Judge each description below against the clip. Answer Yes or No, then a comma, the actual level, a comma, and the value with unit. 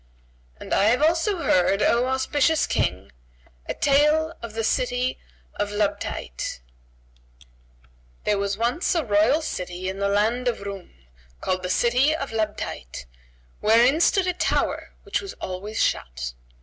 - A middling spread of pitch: No, wide, 7.0 semitones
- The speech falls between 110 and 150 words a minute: Yes, average, 140 wpm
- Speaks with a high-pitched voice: Yes, high, 220 Hz